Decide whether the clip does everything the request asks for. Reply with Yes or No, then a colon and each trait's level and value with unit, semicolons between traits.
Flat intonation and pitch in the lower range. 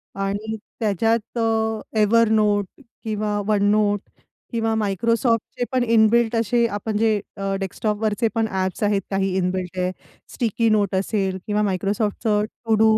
No: narrow, 2.2 semitones; high, 210 Hz